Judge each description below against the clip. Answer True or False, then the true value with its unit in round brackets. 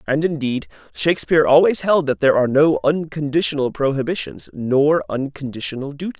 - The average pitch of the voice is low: False (145 Hz)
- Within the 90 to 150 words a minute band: True (135 wpm)